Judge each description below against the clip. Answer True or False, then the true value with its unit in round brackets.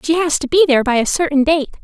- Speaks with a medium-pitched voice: False (295 Hz)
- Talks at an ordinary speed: False (295 wpm)